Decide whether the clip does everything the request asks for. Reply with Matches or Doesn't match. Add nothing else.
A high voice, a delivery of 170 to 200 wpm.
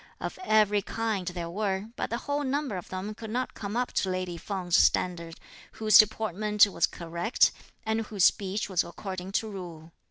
Matches